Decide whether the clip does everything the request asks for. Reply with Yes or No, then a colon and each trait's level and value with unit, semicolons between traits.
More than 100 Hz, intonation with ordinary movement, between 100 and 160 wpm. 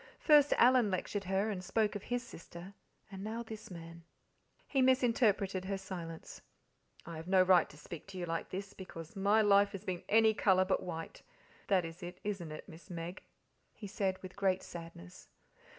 No: high, 190 Hz; average, 3.1 semitones; average, 180 wpm